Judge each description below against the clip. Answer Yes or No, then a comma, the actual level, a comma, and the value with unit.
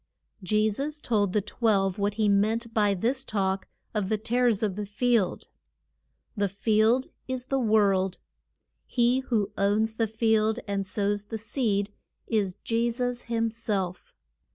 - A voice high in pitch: Yes, high, 215 Hz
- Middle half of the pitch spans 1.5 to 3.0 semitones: Yes, narrow, 2.5 semitones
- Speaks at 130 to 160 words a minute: Yes, average, 150 wpm